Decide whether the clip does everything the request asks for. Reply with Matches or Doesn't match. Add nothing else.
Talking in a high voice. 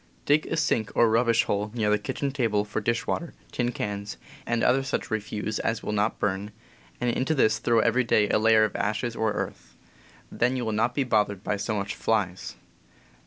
Doesn't match